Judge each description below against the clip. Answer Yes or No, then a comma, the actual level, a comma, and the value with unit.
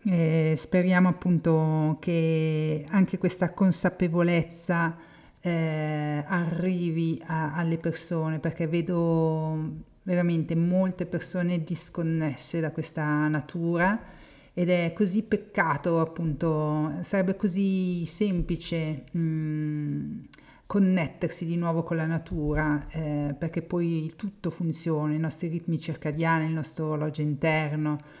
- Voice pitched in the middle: Yes, medium, 165 Hz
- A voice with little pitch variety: Yes, narrow, 2.0 semitones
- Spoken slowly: Yes, slow, 105 wpm